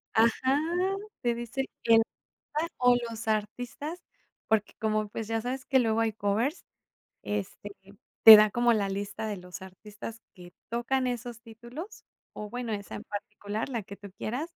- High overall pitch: Yes, high, 225 Hz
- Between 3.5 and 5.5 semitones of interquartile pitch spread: No, average, 2.8 semitones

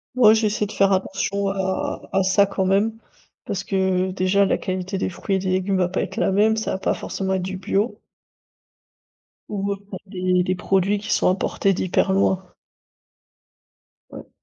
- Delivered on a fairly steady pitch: Yes, narrow, 1.1 semitones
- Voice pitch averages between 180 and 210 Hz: Yes, high, 190 Hz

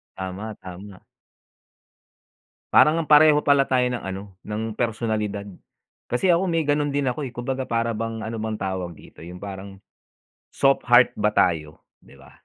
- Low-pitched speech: Yes, low, 110 Hz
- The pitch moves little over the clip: No, wide, 5.5 semitones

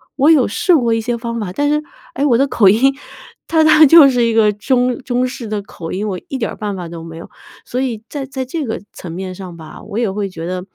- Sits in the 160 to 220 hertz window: No, high, 230 Hz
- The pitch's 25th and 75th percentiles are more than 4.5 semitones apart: Yes, wide, 5.4 semitones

